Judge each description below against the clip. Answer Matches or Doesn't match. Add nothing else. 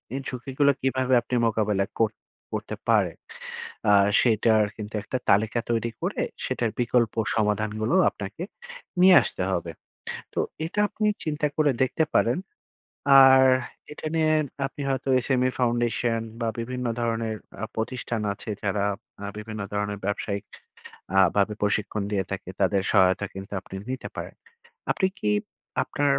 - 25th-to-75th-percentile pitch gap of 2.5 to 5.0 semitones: Matches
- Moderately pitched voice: Doesn't match